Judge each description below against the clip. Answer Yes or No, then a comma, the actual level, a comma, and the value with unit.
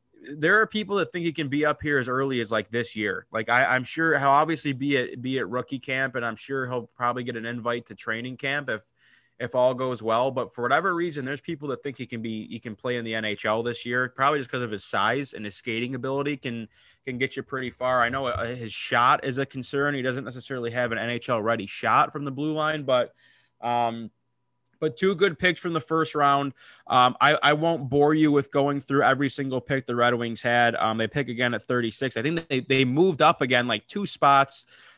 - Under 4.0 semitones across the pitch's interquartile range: Yes, average, 3.1 semitones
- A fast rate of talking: Yes, fast, 240 wpm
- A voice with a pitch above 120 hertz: Yes, low, 130 Hz